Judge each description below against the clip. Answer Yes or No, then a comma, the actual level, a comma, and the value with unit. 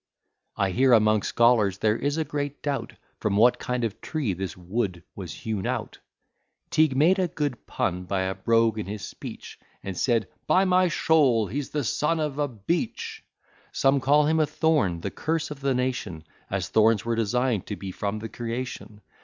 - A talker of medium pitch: No, low, 115 Hz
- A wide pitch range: Yes, wide, 6.2 semitones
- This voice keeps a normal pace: Yes, average, 185 wpm